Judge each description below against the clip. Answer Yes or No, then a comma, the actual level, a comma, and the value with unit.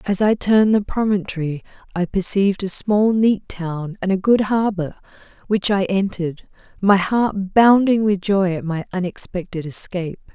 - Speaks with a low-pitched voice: No, high, 195 Hz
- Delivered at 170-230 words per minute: No, average, 155 wpm